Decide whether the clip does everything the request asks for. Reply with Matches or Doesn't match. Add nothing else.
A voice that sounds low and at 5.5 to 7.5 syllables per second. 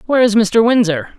Doesn't match